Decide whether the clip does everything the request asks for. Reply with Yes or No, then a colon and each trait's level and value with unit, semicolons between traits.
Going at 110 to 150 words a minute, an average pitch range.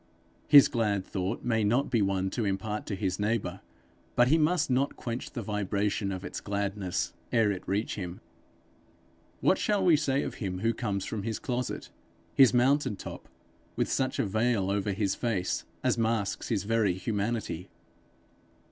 No: average, 165 wpm; average, 3.6 semitones